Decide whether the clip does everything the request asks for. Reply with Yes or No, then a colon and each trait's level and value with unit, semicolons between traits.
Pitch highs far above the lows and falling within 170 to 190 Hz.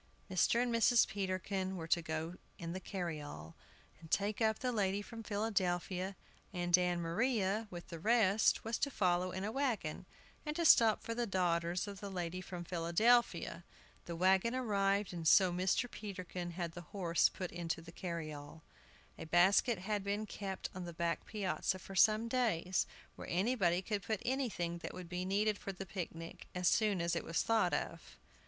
No: average, 3.7 semitones; medium, 185 Hz